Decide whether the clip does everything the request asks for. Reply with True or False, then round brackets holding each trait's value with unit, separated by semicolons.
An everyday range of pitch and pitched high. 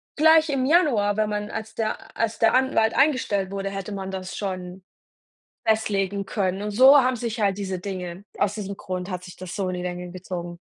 True (3.2 semitones; 200 Hz)